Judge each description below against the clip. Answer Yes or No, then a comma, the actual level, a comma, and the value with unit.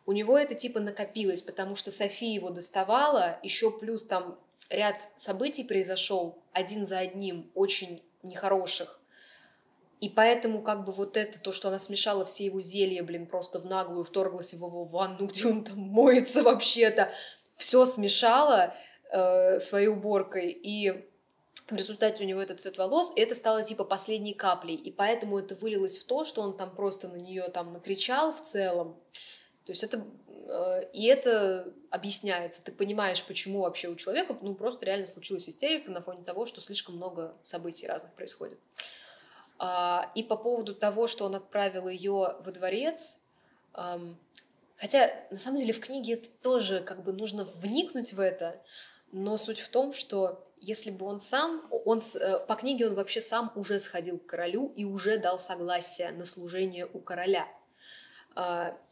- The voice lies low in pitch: No, high, 200 Hz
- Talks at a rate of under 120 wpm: No, fast, 160 wpm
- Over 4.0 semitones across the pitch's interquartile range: No, average, 3.5 semitones